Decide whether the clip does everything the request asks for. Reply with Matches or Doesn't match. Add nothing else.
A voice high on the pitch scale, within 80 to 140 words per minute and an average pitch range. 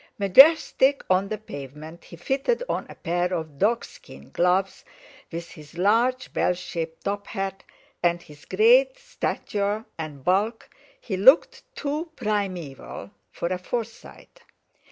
Doesn't match